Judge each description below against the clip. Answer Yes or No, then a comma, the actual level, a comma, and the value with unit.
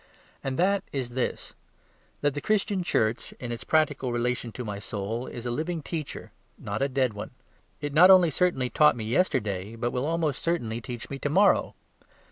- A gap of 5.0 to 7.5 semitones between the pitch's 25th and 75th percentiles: Yes, average, 5.3 semitones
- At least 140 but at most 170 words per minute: No, average, 185 wpm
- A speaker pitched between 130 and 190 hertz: Yes, low, 135 Hz